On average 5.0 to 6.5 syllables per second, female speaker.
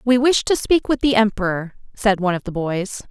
Yes: 5.4 syllables/s; female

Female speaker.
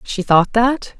Yes: female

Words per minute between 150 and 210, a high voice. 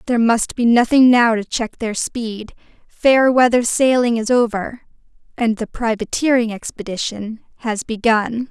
No: average, 140 wpm; high, 230 Hz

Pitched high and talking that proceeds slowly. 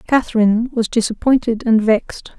Yes: high, 230 Hz; slow, 125 wpm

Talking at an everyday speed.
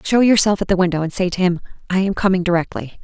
No: fast, 255 wpm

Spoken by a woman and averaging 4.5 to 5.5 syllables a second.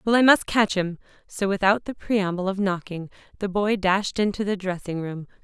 Yes: female; 5.0 syllables/s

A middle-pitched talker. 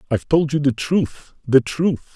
Yes: medium, 145 Hz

